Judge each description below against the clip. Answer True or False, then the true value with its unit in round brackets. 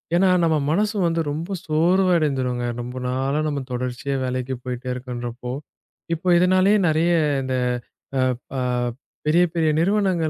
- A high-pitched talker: False (155 Hz)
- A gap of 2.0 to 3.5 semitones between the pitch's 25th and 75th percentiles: False (5.6 semitones)